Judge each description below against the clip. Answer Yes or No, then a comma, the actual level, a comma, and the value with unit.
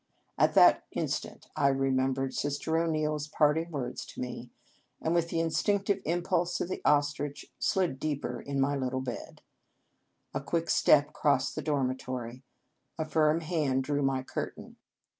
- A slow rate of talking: No, average, 160 wpm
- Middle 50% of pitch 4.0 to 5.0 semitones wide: No, average, 3.3 semitones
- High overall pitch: No, medium, 145 Hz